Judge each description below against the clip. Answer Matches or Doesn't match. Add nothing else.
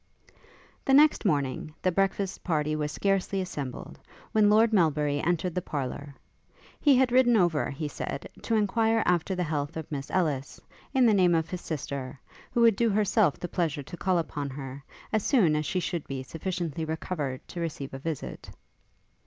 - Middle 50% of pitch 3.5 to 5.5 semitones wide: Matches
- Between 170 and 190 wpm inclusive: Matches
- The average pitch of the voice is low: Doesn't match